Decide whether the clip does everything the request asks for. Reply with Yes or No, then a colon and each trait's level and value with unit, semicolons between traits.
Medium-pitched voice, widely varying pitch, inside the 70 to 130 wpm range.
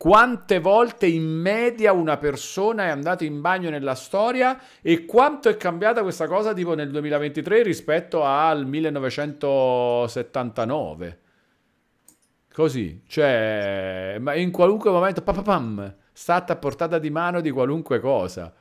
Yes: medium, 160 Hz; wide, 6.7 semitones; average, 125 wpm